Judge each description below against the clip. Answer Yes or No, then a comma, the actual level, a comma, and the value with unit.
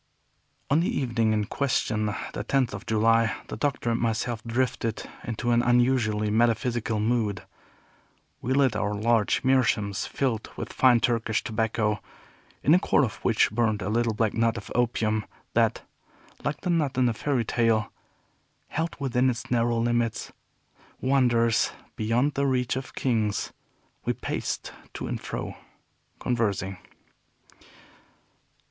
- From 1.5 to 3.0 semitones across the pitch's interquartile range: Yes, narrow, 2.5 semitones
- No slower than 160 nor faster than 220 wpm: No, average, 140 wpm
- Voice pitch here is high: No, low, 115 Hz